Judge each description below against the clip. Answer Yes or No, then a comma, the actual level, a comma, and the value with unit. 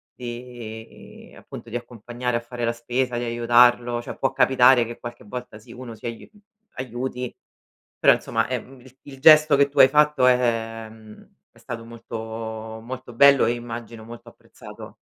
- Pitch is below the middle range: Yes, low, 120 Hz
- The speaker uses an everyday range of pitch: No, narrow, 1.6 semitones